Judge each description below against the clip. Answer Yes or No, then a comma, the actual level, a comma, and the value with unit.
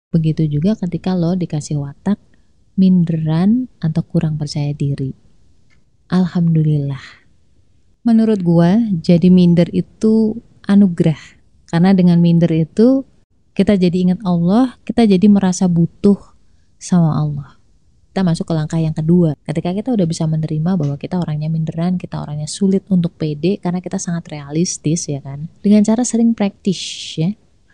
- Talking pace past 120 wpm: Yes, average, 135 wpm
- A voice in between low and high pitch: Yes, medium, 175 Hz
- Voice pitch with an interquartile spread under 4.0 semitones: Yes, average, 3.6 semitones